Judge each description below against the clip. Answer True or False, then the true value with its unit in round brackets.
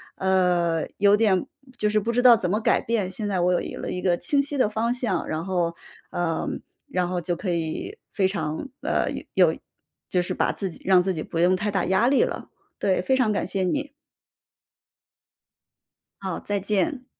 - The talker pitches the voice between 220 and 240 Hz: False (190 Hz)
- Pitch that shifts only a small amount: False (3.4 semitones)